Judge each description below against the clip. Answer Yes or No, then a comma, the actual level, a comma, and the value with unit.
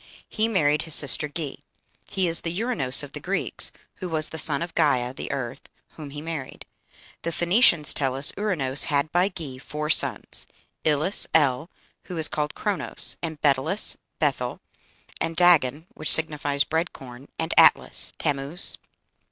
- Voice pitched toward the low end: No, medium, 155 Hz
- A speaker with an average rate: Yes, average, 160 wpm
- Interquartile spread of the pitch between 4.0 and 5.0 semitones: No, average, 3.3 semitones